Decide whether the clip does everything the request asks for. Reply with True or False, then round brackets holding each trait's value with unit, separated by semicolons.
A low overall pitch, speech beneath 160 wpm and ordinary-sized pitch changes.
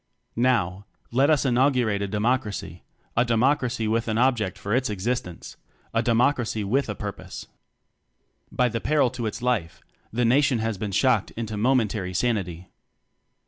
True (115 Hz; 150 wpm; 3.5 semitones)